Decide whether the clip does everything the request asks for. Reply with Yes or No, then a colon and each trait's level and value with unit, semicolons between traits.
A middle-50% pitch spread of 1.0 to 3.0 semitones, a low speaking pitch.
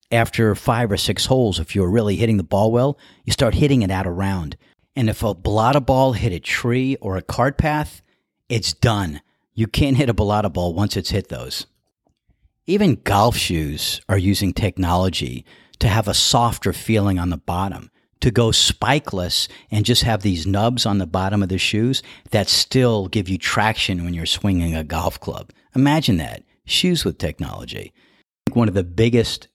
No: average, 4.3 semitones; low, 105 Hz